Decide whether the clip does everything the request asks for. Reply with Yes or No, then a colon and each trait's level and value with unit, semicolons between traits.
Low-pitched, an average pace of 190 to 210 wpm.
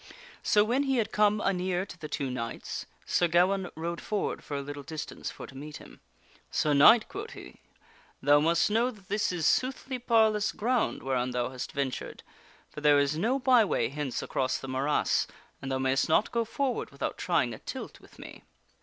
No: medium, 170 Hz; average, 200 wpm